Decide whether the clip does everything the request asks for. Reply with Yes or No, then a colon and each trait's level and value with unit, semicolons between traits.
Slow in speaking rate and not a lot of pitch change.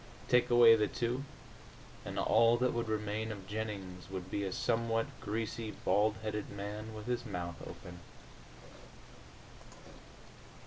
Yes: slow, 130 wpm; narrow, 2.2 semitones